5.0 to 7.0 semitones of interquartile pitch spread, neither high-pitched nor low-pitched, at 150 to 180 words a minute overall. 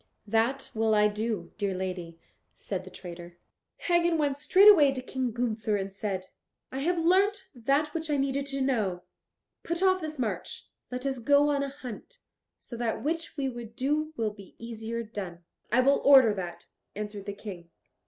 No: wide, 5.6 semitones; high, 245 Hz; average, 175 wpm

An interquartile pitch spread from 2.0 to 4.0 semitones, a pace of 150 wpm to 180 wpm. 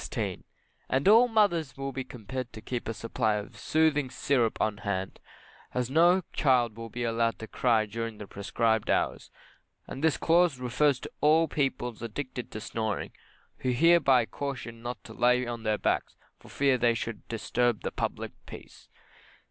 Yes: average, 3.6 semitones; average, 170 wpm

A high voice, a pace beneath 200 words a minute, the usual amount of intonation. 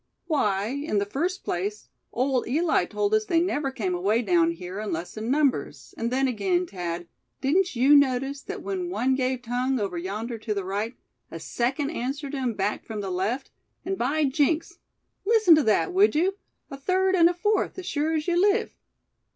No: very high, 270 Hz; average, 190 wpm; wide, 7.9 semitones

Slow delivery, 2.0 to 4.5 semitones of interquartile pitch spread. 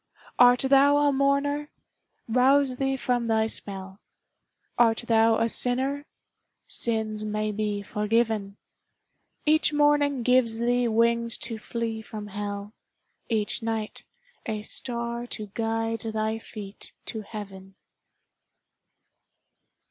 Yes: slow, 110 wpm; average, 2.8 semitones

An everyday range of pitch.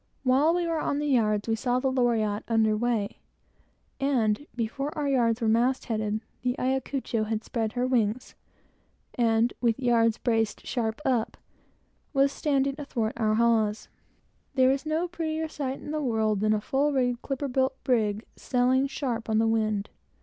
Yes: average, 3.5 semitones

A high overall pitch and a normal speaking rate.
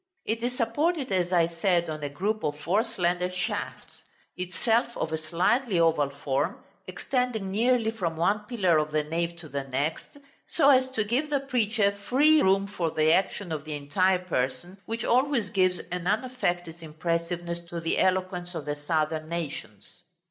No: medium, 180 Hz; average, 170 wpm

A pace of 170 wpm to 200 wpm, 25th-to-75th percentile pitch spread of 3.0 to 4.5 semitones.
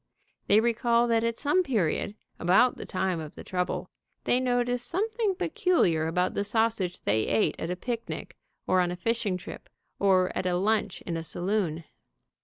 No: average, 175 wpm; average, 5.0 semitones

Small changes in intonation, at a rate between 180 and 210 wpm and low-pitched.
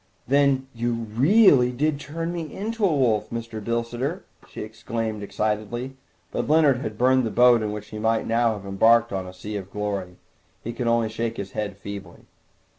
No: average, 3.7 semitones; average, 185 wpm; low, 115 Hz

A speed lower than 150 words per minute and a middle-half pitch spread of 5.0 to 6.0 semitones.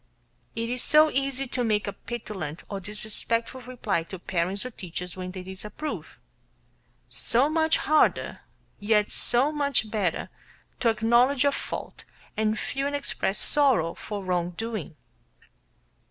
Yes: average, 140 wpm; wide, 5.5 semitones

